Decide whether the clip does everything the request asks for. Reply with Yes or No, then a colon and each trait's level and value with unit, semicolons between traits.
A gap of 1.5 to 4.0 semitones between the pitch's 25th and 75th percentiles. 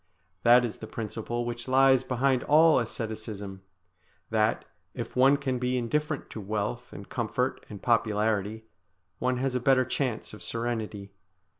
Yes: average, 2.9 semitones